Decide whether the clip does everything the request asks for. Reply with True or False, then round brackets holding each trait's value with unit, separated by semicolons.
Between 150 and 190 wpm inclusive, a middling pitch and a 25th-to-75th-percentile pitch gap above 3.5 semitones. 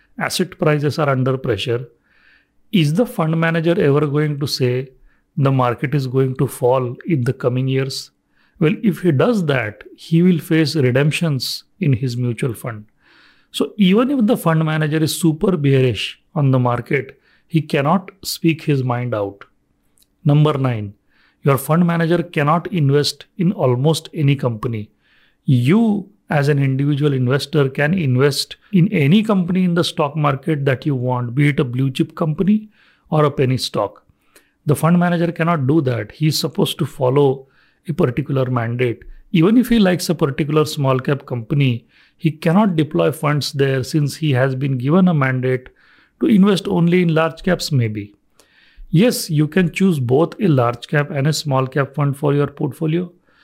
True (170 wpm; 150 Hz; 4.1 semitones)